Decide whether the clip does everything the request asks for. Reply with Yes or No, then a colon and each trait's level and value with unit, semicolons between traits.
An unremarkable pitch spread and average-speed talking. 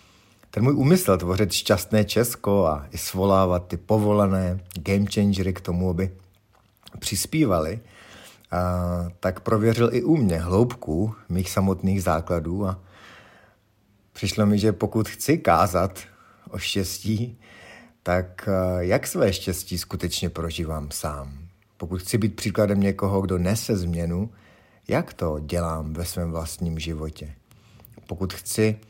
Yes: average, 3.2 semitones; average, 125 wpm